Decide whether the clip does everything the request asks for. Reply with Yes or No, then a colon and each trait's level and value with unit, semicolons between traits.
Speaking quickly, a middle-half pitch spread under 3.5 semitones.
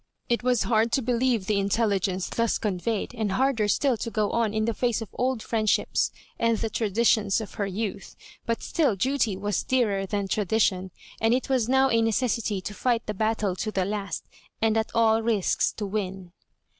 No: average, 190 wpm; narrow, 2.6 semitones